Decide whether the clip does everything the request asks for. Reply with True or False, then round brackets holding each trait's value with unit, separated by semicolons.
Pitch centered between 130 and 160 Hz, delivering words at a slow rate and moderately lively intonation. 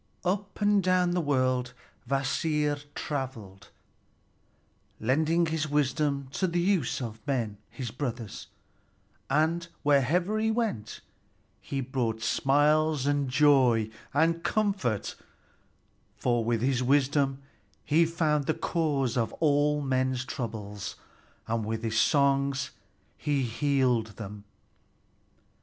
True (140 Hz; 110 wpm; 4.1 semitones)